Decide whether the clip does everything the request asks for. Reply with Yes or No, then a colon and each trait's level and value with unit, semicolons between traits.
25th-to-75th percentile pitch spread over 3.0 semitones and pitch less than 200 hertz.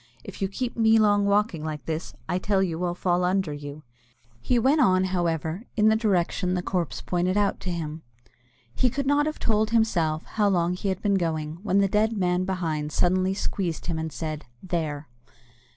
Yes: average, 4.0 semitones; medium, 185 Hz